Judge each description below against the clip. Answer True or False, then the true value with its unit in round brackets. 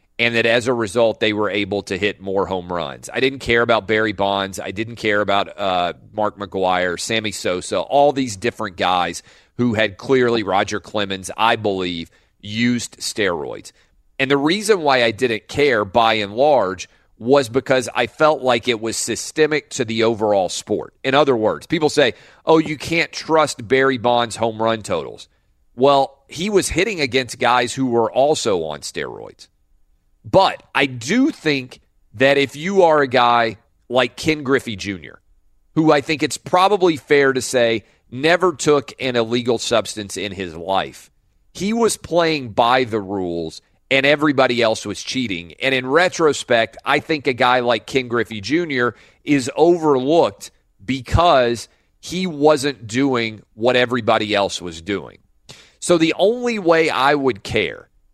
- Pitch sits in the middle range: False (120 Hz)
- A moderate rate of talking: True (165 wpm)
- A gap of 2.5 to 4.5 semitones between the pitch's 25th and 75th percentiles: False (5.2 semitones)